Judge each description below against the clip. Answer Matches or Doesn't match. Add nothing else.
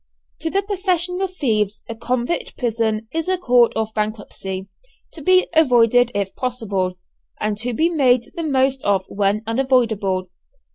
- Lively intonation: Matches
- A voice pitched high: Matches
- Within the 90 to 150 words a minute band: Matches